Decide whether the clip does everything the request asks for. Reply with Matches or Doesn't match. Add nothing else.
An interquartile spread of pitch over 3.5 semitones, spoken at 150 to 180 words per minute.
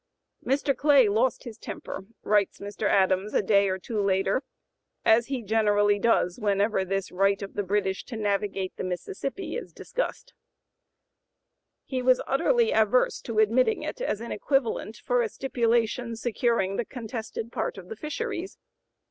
Matches